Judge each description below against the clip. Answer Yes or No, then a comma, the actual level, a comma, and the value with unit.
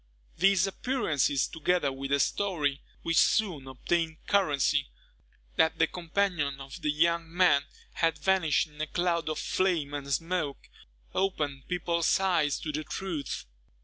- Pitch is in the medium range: Yes, medium, 160 Hz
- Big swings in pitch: No, average, 3.9 semitones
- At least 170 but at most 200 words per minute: No, average, 140 wpm